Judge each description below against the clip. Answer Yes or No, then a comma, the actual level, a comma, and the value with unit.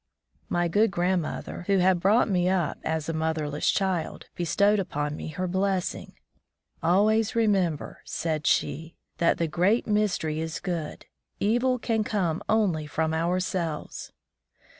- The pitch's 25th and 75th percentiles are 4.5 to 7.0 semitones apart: No, average, 3.9 semitones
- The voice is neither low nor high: Yes, medium, 180 Hz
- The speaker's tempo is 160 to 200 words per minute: No, average, 140 wpm